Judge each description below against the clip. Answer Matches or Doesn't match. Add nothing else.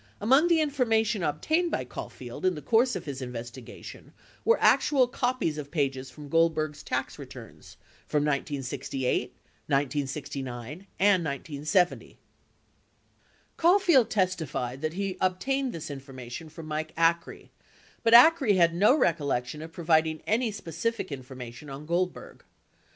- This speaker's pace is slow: Matches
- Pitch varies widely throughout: Matches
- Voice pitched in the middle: Matches